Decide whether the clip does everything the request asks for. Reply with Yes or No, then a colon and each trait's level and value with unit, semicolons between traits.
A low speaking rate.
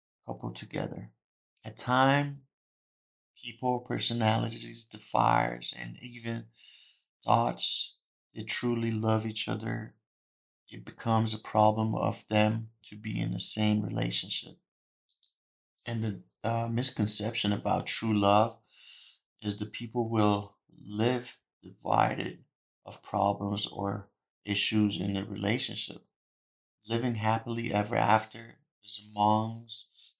Yes: slow, 105 wpm